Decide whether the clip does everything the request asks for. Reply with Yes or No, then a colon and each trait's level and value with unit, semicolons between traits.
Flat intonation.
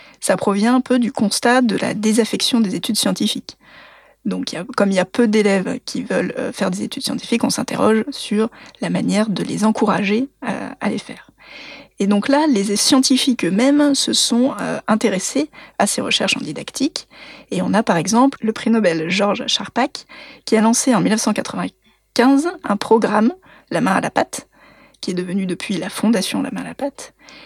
No: average, 4.2 semitones